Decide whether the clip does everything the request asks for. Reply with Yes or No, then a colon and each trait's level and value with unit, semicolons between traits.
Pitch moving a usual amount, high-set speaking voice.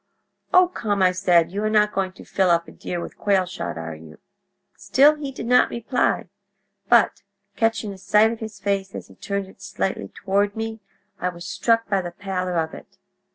Yes: average, 3.3 semitones; high, 200 Hz